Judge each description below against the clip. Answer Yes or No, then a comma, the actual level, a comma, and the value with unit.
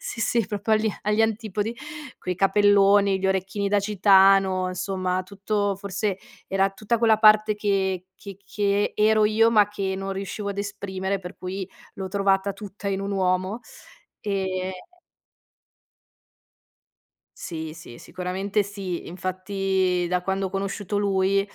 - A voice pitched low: No, high, 195 Hz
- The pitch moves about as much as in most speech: No, narrow, 1.5 semitones